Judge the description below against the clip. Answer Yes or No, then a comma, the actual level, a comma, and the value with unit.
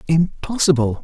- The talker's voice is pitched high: No, medium, 150 Hz